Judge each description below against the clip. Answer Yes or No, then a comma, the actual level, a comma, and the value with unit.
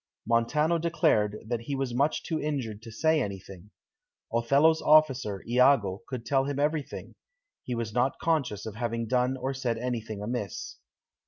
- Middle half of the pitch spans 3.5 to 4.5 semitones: Yes, average, 4.2 semitones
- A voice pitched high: No, low, 125 Hz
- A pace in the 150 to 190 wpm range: Yes, average, 155 wpm